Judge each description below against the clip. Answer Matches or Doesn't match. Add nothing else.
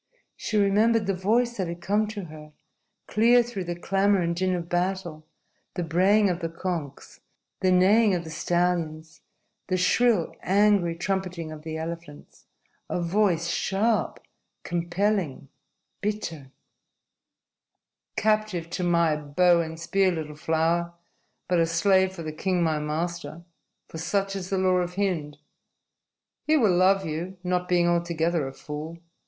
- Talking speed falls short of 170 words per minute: Matches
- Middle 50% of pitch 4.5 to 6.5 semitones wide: Doesn't match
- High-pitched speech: Doesn't match